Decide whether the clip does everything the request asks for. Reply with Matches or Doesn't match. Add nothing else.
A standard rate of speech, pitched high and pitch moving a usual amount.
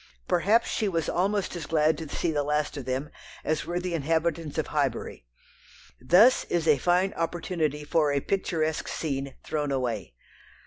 Doesn't match